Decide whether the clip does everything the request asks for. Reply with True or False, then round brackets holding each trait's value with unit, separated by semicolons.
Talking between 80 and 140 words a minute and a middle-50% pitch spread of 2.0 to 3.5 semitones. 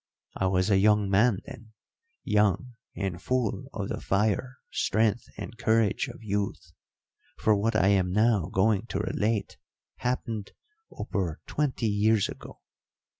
True (135 wpm; 2.5 semitones)